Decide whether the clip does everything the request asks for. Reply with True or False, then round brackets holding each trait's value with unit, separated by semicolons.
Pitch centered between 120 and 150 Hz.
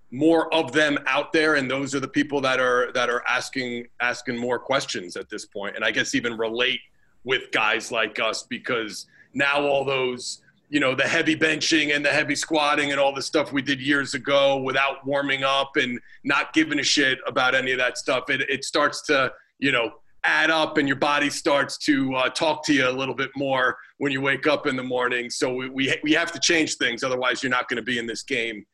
True (140 Hz)